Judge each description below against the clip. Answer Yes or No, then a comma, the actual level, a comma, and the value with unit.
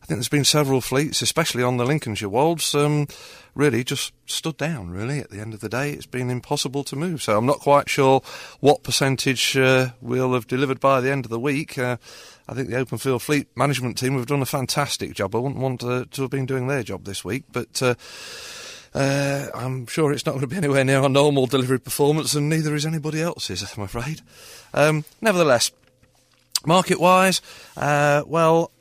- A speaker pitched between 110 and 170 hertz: Yes, low, 135 Hz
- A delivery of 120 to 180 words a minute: No, fast, 205 wpm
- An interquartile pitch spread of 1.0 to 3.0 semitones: Yes, average, 2.7 semitones